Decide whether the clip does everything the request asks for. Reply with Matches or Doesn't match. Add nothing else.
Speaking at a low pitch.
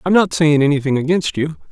Doesn't match